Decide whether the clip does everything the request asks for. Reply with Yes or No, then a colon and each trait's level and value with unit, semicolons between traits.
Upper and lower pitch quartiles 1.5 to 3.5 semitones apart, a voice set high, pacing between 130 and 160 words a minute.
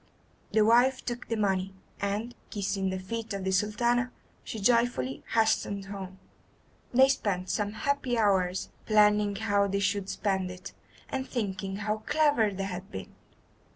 Yes: average, 3.0 semitones; high, 205 Hz; average, 150 wpm